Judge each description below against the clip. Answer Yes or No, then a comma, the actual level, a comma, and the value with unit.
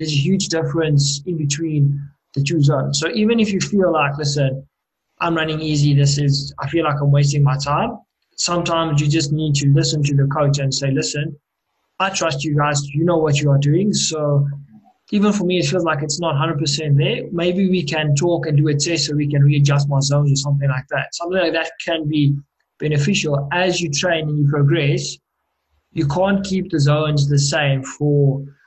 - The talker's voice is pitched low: No, medium, 150 Hz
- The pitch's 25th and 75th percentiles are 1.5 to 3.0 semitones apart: Yes, narrow, 2.6 semitones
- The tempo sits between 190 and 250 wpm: Yes, fast, 205 wpm